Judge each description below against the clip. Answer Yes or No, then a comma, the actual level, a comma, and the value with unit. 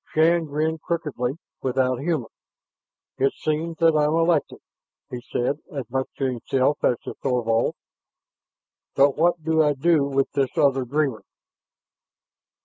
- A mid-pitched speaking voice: Yes, medium, 145 Hz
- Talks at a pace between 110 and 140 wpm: Yes, slow, 135 wpm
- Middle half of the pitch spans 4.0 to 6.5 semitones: No, average, 3.4 semitones